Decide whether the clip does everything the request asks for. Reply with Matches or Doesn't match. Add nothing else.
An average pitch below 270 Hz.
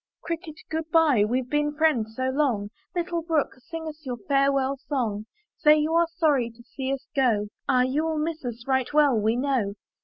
Doesn't match